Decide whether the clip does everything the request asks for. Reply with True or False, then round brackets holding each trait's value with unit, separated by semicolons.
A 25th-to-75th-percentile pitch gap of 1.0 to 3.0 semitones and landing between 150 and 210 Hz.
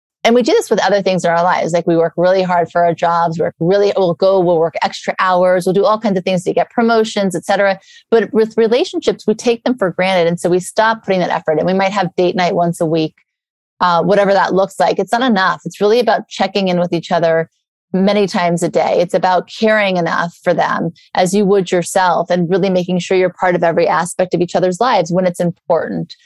True (2.6 semitones; 185 Hz)